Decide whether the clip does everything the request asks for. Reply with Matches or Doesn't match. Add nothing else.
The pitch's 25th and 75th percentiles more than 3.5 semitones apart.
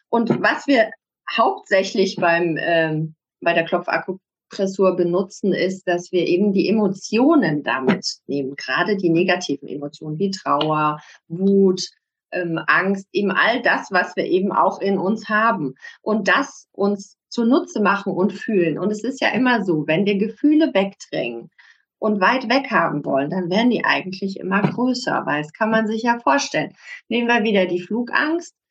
Matches